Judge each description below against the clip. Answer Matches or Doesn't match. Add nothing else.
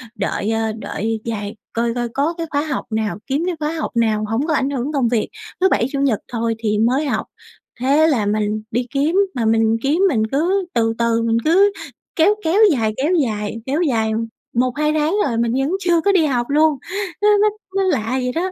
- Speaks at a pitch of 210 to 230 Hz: Doesn't match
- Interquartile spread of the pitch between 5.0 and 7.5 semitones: Matches